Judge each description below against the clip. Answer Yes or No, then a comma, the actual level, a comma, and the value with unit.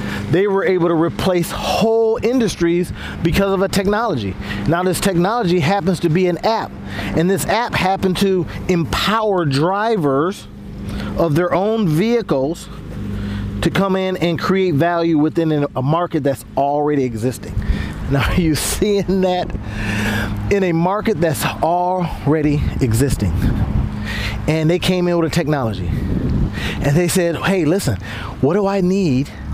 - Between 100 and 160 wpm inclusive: Yes, average, 140 wpm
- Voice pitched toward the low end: No, medium, 170 Hz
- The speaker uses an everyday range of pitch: No, wide, 6.6 semitones